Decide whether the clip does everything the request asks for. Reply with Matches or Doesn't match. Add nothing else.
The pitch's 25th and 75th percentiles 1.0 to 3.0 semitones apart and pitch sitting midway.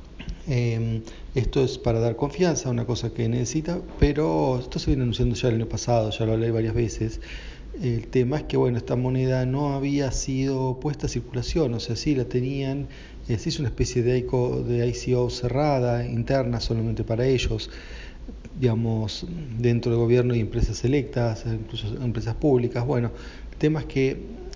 Doesn't match